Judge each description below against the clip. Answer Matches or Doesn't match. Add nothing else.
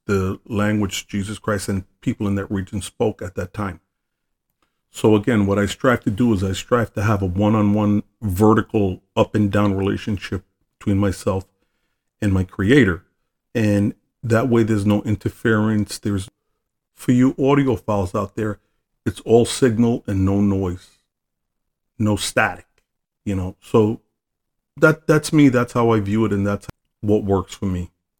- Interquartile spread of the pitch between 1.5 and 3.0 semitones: Matches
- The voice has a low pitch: Matches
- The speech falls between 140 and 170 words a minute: Matches